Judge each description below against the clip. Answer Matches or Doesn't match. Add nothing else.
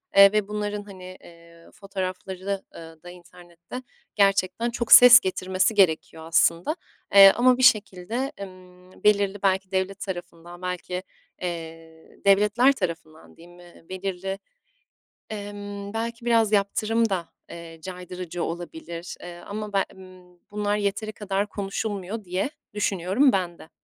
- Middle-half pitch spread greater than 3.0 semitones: Doesn't match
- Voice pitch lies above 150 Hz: Matches